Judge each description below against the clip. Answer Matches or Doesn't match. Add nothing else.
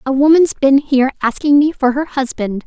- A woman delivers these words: Matches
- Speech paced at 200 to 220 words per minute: Matches